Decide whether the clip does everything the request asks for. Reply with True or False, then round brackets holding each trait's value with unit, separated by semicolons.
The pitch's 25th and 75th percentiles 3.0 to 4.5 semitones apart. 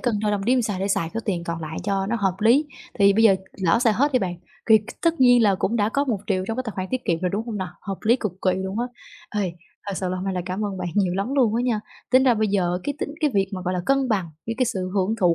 True (4.1 semitones)